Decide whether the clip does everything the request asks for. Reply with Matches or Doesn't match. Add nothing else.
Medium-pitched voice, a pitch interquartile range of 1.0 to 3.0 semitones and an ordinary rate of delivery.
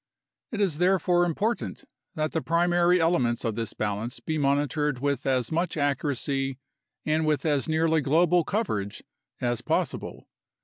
Doesn't match